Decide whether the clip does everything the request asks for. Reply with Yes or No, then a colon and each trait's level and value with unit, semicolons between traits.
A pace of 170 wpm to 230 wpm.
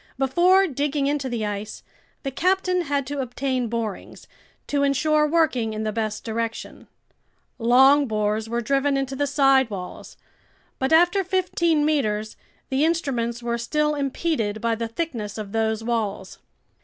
No: average, 145 wpm